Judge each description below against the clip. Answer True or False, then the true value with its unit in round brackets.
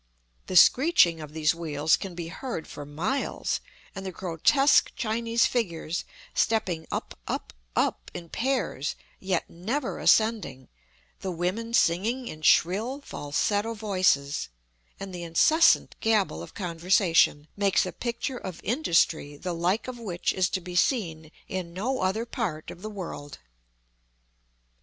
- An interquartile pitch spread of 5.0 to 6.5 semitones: True (5.6 semitones)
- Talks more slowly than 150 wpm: True (140 wpm)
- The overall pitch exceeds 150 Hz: True (185 Hz)